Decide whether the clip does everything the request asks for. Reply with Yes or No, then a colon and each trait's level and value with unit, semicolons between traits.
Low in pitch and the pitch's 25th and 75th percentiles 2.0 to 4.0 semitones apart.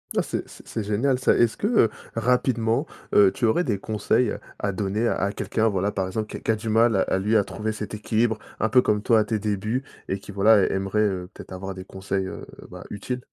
Yes: low, 105 Hz; narrow, 2.5 semitones